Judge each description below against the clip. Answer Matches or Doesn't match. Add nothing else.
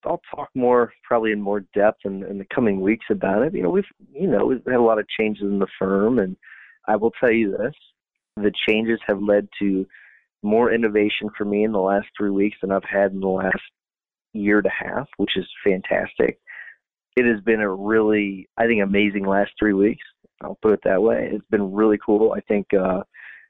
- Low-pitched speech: Matches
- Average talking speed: Doesn't match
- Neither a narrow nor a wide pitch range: Doesn't match